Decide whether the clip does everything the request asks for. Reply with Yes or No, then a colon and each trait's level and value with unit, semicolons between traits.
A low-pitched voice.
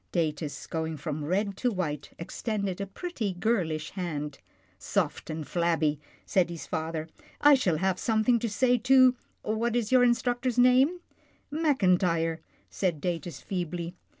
No: medium, 185 Hz